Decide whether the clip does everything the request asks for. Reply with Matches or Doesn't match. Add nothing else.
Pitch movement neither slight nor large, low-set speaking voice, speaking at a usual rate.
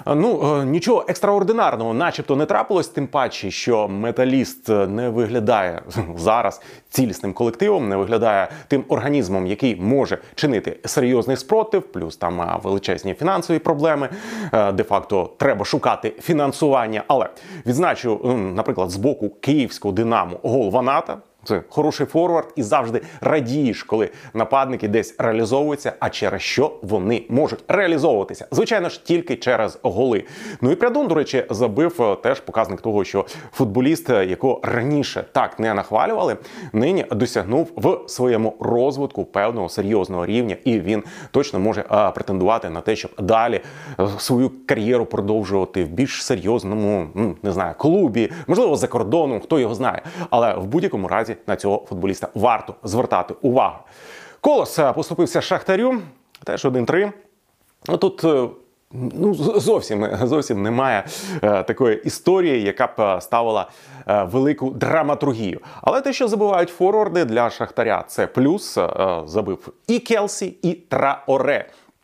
Doesn't match